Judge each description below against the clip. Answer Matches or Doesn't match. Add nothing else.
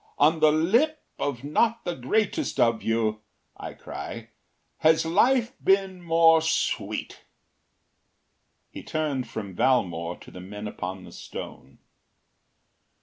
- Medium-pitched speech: Matches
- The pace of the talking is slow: Matches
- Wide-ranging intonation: Matches